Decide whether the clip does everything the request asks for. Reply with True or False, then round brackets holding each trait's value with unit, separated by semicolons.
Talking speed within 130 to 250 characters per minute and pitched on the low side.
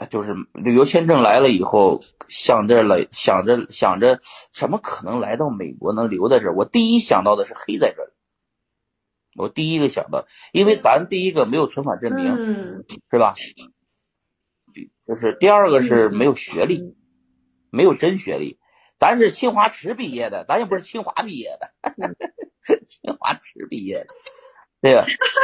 False (235 characters per minute; 210 Hz)